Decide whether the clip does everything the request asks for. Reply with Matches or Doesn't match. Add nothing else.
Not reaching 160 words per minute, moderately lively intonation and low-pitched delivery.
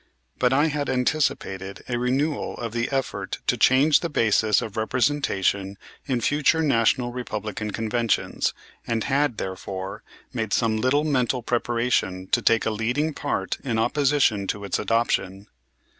Matches